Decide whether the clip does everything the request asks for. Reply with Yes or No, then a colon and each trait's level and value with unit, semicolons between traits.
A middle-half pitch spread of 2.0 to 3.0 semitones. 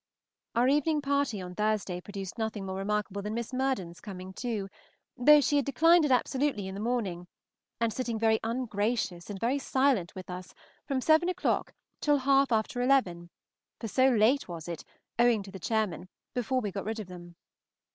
No: wide, 5.4 semitones